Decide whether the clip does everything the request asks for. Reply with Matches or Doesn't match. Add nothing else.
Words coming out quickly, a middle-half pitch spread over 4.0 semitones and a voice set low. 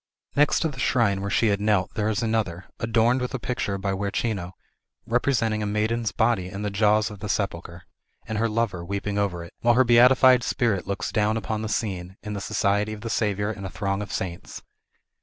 Doesn't match